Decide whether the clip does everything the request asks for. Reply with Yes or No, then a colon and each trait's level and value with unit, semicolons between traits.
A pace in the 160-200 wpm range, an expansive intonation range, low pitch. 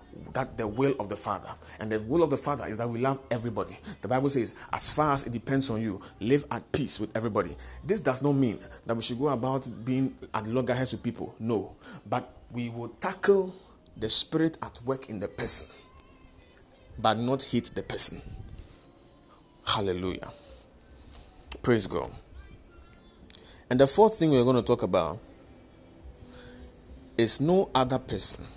Yes: average, 165 wpm; wide, 6.4 semitones; low, 120 Hz